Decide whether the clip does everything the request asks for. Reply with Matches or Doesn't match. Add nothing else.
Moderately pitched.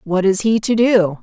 Doesn't match